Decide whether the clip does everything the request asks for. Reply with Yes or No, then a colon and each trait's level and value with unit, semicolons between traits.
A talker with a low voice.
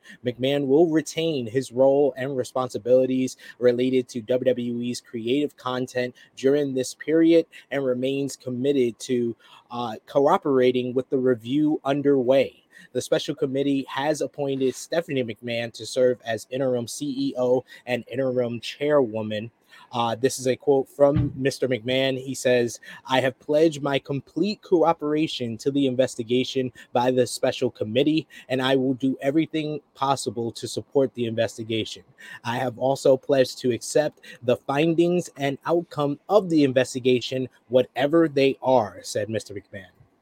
Yes: low, 130 Hz